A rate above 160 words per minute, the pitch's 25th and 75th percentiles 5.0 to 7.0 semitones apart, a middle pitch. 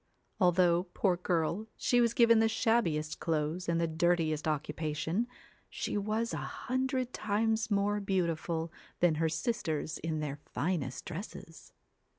No: slow, 135 wpm; average, 5.3 semitones; medium, 175 Hz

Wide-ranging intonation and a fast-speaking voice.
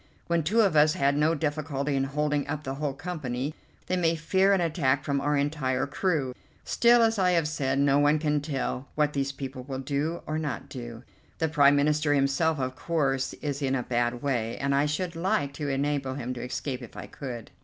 No: narrow, 2.6 semitones; fast, 210 wpm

